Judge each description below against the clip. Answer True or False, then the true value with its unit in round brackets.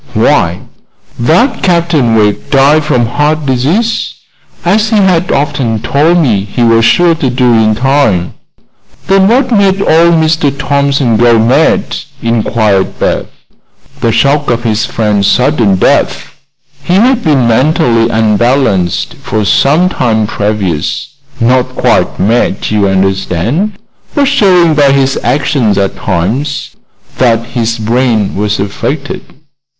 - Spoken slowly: True (130 wpm)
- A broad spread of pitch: True (6.0 semitones)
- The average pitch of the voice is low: True (130 Hz)